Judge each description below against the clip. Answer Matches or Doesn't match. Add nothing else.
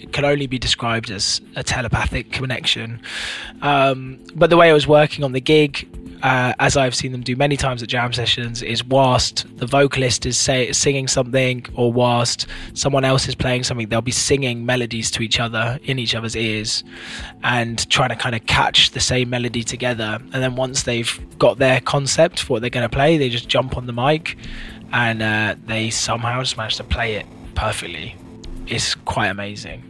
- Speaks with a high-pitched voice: Doesn't match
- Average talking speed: Matches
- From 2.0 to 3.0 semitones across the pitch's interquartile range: Matches